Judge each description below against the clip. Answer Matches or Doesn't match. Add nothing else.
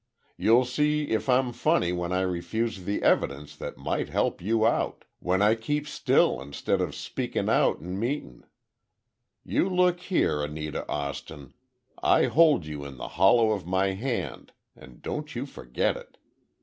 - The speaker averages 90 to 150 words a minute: Doesn't match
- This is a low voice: Matches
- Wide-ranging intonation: Matches